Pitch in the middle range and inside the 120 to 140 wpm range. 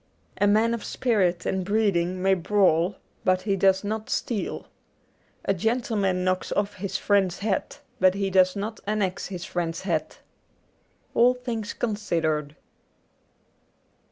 No: high, 195 Hz; slow, 135 wpm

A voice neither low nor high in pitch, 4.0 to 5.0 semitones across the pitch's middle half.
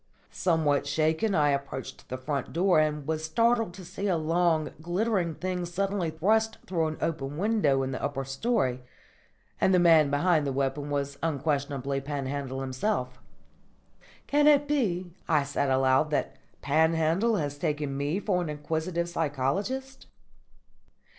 Yes: medium, 155 Hz; average, 4.6 semitones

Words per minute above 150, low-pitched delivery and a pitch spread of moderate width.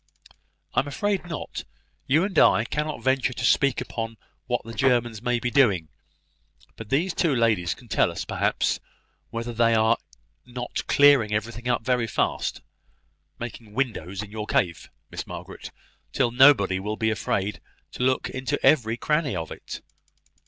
Yes: average, 160 wpm; low, 120 Hz; average, 3.6 semitones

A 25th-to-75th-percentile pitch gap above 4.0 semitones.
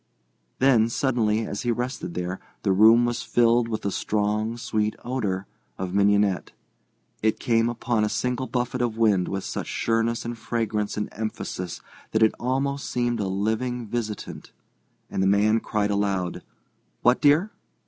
No: average, 2.8 semitones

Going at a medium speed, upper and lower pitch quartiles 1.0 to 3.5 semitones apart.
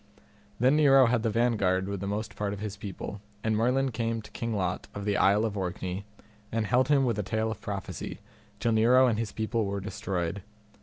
No: fast, 210 wpm; narrow, 2.6 semitones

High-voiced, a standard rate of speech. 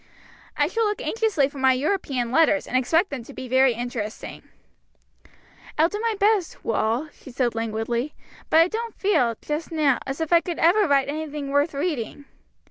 Yes: very high, 285 Hz; average, 180 wpm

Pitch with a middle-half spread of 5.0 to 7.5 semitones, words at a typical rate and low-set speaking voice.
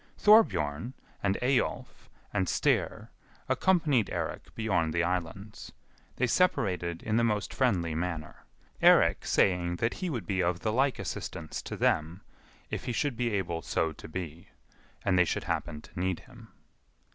Yes: wide, 5.4 semitones; average, 155 wpm; very low, 95 Hz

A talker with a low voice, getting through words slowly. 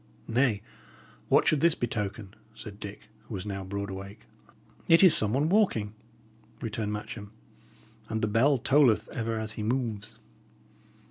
No: low, 110 Hz; average, 145 wpm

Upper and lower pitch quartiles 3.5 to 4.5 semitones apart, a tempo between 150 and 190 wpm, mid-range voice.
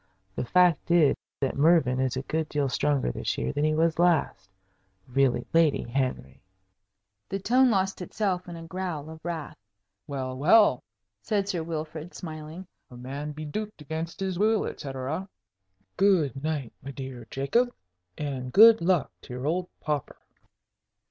No: average, 4.9 semitones; average, 155 wpm; medium, 155 Hz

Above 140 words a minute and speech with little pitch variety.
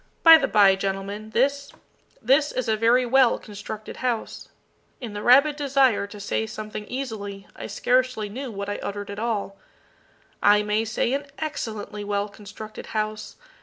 No: average, 160 wpm; average, 3.8 semitones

